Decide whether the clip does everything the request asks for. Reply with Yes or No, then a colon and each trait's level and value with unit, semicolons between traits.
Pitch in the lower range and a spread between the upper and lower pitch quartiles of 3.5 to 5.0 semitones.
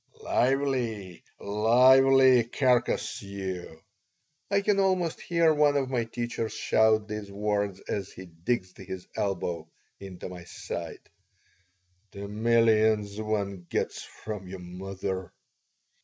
Yes: low, 105 Hz; average, 4.5 semitones